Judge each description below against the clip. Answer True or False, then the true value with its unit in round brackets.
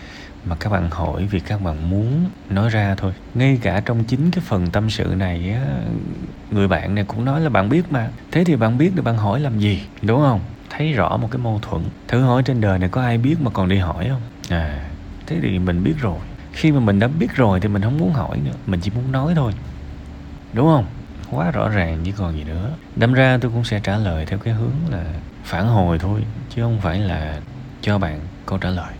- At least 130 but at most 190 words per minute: False (240 wpm)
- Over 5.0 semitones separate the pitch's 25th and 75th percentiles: True (5.5 semitones)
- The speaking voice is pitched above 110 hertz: False (105 Hz)